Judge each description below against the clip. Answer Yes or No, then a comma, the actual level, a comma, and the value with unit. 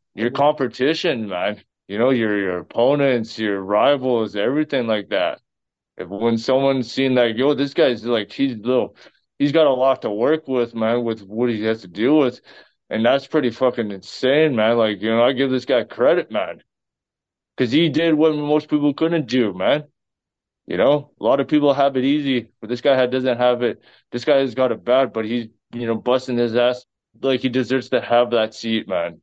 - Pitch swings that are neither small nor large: Yes, average, 3.3 semitones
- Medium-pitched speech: No, low, 125 Hz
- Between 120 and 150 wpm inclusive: No, fast, 205 wpm